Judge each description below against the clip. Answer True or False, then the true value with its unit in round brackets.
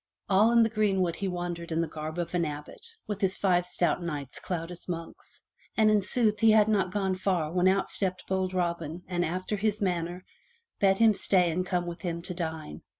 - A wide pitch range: False (2.7 semitones)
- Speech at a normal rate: False (210 wpm)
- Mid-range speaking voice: True (180 Hz)